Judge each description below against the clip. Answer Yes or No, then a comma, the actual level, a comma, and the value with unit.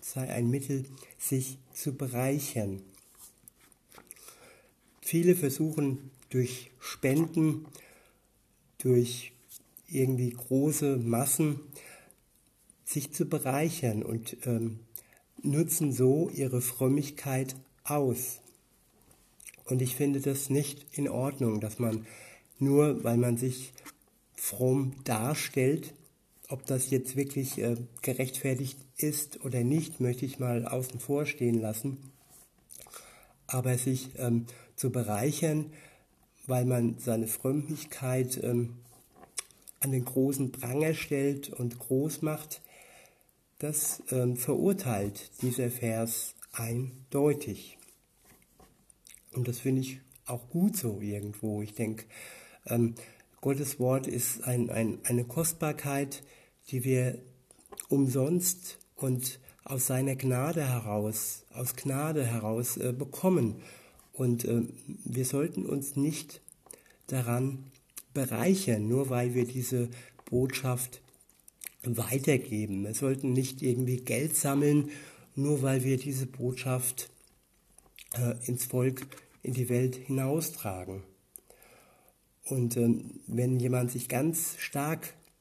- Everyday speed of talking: No, slow, 105 wpm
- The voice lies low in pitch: Yes, low, 130 Hz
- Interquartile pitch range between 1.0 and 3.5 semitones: Yes, narrow, 2.6 semitones